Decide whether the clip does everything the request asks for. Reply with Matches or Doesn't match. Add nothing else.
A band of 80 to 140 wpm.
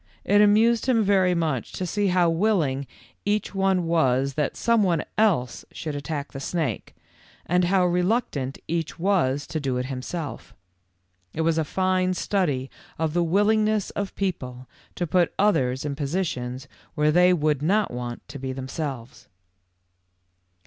Doesn't match